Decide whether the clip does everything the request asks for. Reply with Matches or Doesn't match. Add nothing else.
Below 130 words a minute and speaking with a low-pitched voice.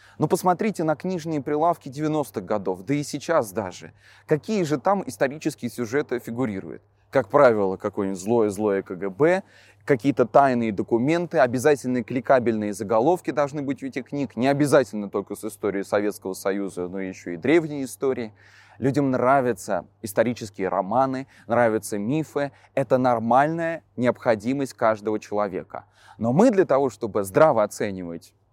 Doesn't match